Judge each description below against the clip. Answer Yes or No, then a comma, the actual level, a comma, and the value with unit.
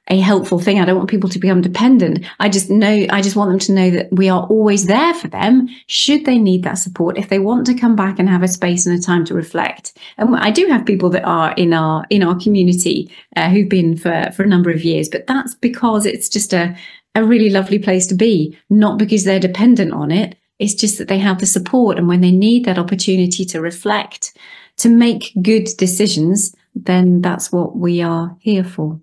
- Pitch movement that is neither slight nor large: Yes, average, 3.0 semitones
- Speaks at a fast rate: Yes, fast, 230 wpm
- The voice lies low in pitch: No, high, 195 Hz